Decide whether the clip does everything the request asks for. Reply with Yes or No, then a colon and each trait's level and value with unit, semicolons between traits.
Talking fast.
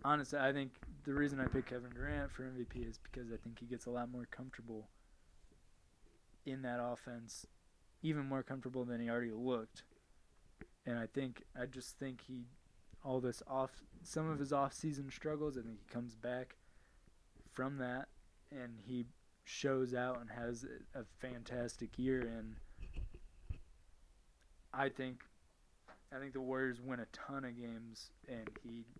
No: average, 160 wpm